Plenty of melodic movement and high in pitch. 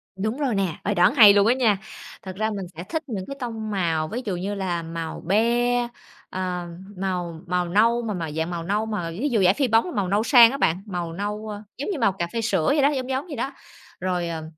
No: average, 4.8 semitones; high, 205 Hz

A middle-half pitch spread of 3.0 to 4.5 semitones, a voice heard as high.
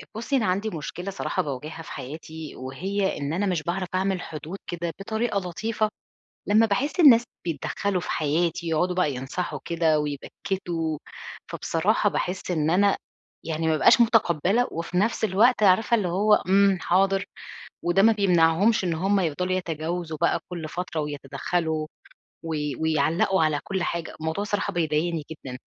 No: average, 3.7 semitones; medium, 175 Hz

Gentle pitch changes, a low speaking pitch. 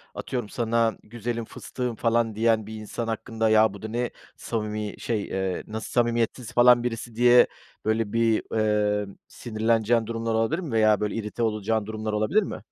Yes: narrow, 1.5 semitones; low, 110 Hz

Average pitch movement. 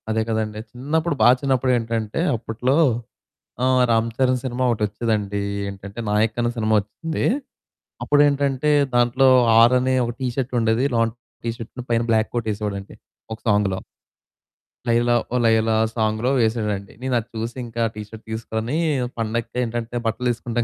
No: narrow, 2.2 semitones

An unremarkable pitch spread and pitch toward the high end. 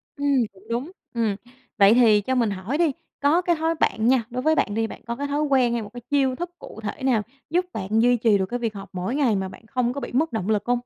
Yes: average, 4.6 semitones; high, 245 Hz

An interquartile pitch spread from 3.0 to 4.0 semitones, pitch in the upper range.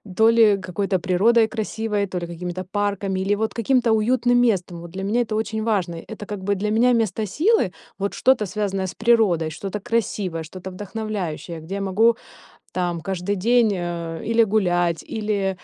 Yes: average, 3.4 semitones; high, 200 Hz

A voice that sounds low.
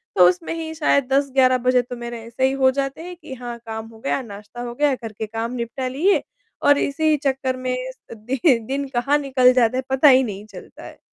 No: very high, 255 Hz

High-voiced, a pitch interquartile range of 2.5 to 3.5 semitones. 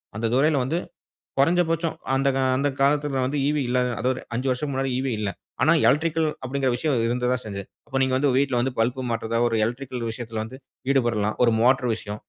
No: low, 130 Hz; average, 2.9 semitones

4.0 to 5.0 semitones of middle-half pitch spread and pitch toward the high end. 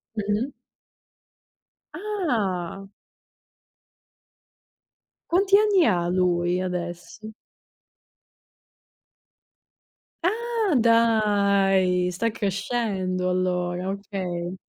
Yes: average, 4.3 semitones; high, 195 Hz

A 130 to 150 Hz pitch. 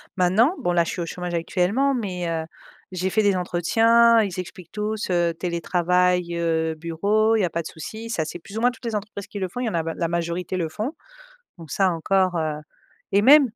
No: medium, 180 Hz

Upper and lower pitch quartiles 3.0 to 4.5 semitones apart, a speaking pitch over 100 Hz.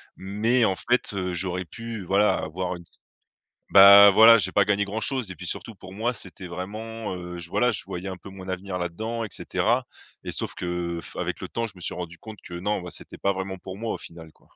No: average, 3.4 semitones; very low, 95 Hz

